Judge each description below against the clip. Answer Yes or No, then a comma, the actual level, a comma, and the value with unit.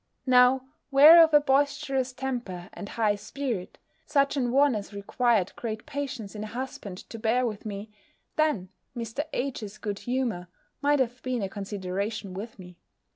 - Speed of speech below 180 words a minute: Yes, average, 165 wpm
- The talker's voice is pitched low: No, high, 235 Hz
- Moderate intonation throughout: Yes, average, 4.6 semitones